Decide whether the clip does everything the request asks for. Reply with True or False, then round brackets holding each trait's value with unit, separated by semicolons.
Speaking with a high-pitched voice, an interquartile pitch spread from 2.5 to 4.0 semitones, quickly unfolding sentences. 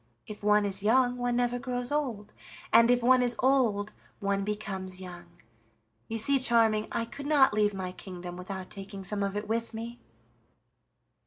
False (215 Hz; 3.6 semitones; 170 wpm)